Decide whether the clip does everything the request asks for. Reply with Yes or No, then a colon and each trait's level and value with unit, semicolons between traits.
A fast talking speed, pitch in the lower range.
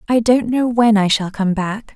No: fast, 245 wpm; high, 220 Hz